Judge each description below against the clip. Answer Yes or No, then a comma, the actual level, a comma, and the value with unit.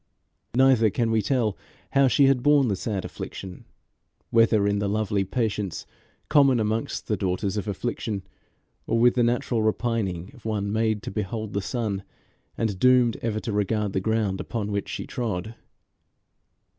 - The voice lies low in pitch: Yes, low, 110 Hz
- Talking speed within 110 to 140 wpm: No, average, 160 wpm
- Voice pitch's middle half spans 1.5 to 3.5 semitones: Yes, average, 2.8 semitones